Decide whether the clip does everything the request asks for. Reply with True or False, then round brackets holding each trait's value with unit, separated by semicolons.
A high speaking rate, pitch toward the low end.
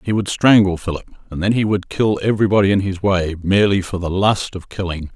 True (220 wpm; 95 Hz)